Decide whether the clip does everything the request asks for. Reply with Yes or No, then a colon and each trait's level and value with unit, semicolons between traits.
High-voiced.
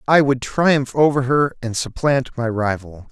No: low, 130 Hz